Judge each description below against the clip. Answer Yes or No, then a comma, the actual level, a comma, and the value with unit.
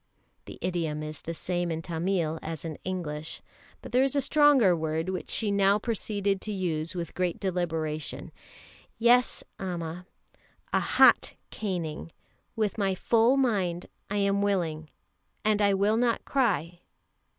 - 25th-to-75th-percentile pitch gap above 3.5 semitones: Yes, average, 4.1 semitones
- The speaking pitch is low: No, medium, 185 Hz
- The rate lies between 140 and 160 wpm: Yes, average, 145 wpm